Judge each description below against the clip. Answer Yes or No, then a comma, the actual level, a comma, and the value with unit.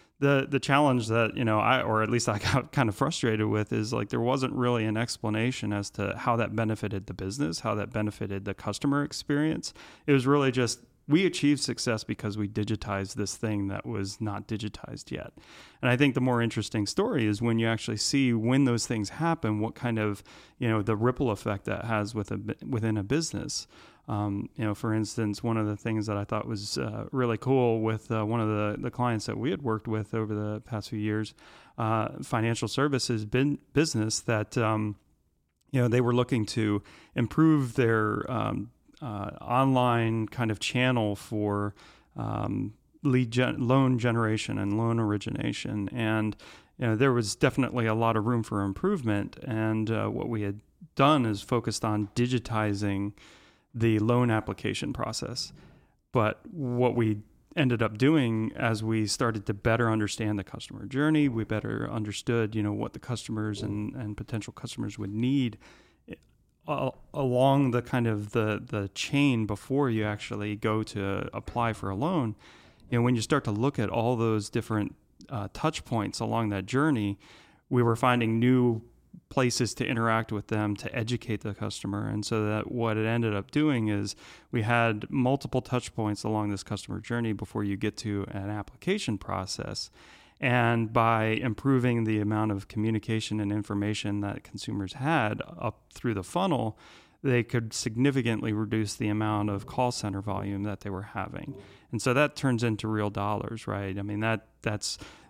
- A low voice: Yes, low, 110 Hz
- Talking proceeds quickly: No, average, 180 wpm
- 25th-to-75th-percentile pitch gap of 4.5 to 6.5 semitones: No, average, 2.9 semitones